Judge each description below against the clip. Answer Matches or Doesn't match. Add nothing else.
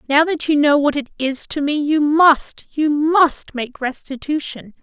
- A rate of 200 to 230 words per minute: Doesn't match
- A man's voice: Doesn't match